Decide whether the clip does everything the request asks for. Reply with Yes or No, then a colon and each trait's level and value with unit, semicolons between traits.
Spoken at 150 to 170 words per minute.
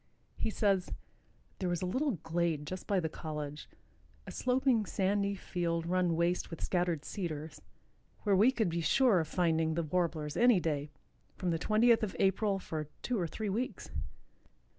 Yes: average, 165 wpm